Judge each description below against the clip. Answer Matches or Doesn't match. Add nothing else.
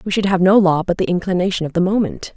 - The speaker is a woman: Matches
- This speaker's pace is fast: Matches